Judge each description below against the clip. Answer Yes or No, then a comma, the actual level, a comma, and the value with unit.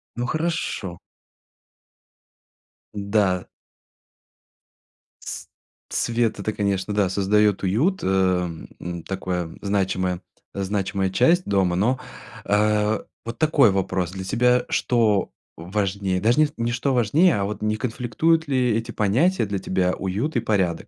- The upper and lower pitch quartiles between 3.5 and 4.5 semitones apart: Yes, average, 4.0 semitones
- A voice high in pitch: No, low, 105 Hz